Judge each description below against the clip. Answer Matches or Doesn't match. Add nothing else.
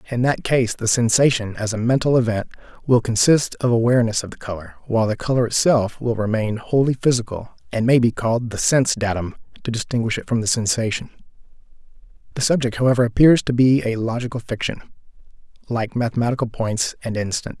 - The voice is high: Doesn't match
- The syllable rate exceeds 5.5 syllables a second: Matches